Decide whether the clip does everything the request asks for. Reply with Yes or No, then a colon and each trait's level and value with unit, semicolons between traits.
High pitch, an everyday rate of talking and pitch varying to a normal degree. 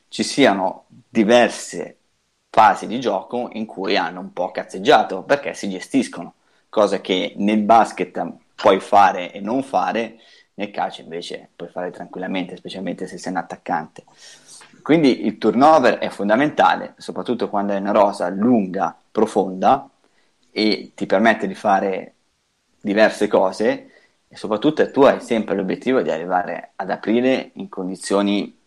No: low, 105 Hz; average, 140 wpm; average, 3.1 semitones